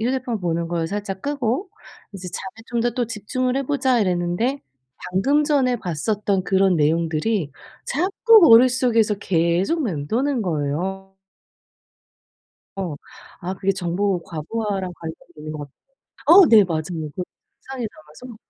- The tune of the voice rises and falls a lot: Yes, wide, 6.4 semitones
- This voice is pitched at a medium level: No, high, 195 Hz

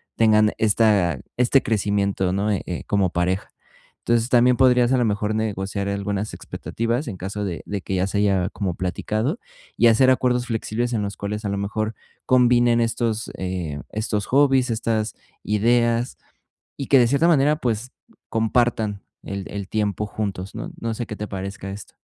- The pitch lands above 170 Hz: No, low, 110 Hz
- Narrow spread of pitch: No, average, 3.1 semitones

